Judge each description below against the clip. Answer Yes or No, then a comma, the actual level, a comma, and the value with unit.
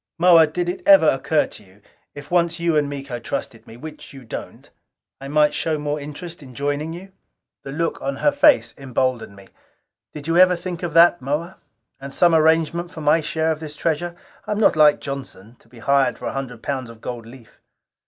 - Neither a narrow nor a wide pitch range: Yes, average, 3.8 semitones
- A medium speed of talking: No, fast, 210 wpm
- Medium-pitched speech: Yes, medium, 150 Hz